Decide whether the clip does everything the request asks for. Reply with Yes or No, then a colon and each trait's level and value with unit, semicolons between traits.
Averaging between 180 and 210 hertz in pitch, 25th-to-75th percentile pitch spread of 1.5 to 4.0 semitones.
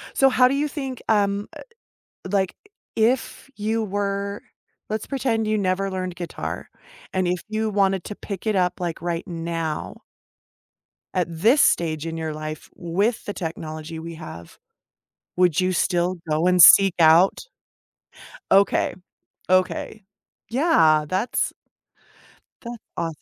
No: medium, 185 Hz; average, 4.4 semitones